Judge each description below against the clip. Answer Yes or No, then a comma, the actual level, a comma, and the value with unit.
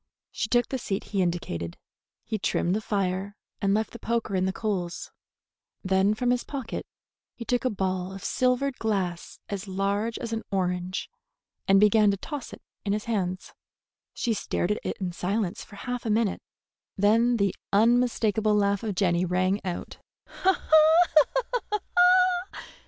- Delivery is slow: No, average, 155 wpm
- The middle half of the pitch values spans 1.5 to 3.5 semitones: Yes, average, 3.2 semitones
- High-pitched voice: Yes, high, 200 Hz